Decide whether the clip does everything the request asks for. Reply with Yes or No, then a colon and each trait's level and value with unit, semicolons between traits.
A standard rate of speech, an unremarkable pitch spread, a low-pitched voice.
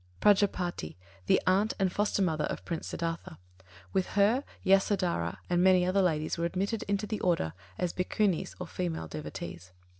No: average, 155 wpm; average, 3.2 semitones; medium, 180 Hz